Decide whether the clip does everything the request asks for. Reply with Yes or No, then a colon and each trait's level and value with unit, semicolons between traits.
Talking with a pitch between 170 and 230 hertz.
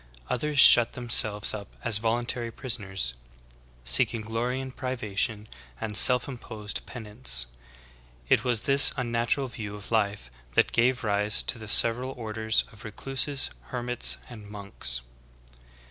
No: low, 115 Hz